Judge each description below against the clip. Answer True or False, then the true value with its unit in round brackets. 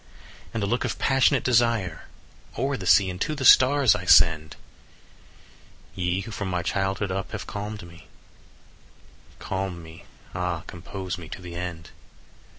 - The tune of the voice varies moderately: True (3.5 semitones)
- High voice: False (95 Hz)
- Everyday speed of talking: True (155 wpm)